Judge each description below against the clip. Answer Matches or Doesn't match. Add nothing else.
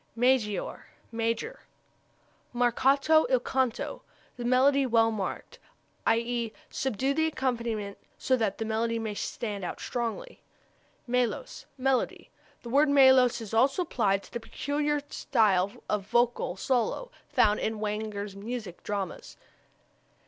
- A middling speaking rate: Doesn't match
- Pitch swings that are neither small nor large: Matches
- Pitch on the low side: Doesn't match